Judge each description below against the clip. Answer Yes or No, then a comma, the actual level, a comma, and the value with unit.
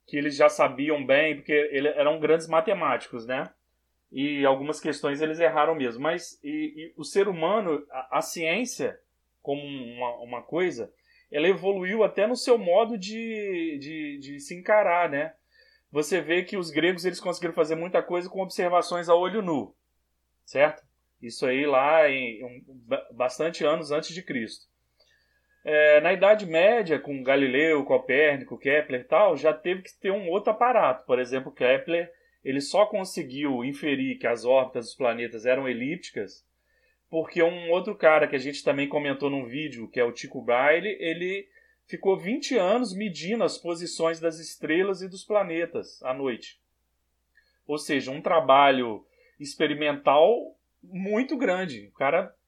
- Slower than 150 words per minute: No, average, 155 wpm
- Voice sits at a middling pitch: Yes, medium, 155 Hz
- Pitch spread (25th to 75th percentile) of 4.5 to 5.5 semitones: Yes, average, 5.2 semitones